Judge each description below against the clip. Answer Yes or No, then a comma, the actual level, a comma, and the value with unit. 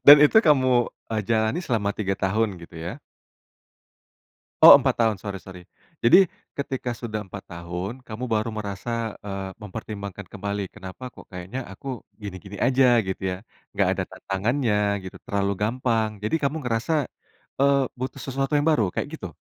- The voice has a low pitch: Yes, low, 110 Hz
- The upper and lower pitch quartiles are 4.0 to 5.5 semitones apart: Yes, average, 4.5 semitones